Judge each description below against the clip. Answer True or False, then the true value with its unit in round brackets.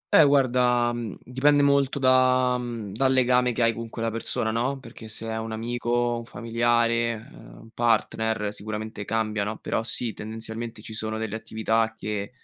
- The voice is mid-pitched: False (115 Hz)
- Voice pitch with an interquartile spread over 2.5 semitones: False (1.8 semitones)